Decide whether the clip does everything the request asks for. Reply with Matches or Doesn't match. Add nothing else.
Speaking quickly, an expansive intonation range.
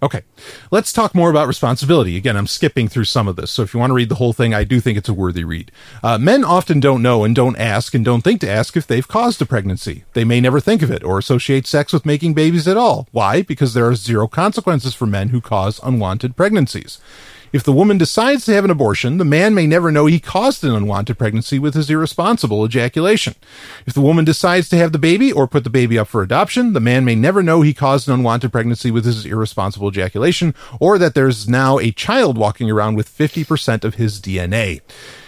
Matches